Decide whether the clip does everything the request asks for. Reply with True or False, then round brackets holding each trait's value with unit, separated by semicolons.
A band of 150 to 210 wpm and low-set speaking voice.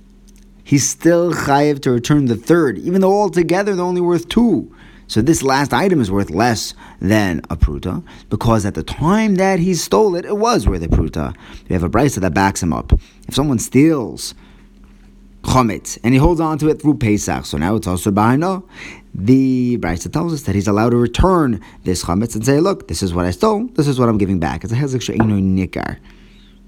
True (205 wpm; 120 Hz)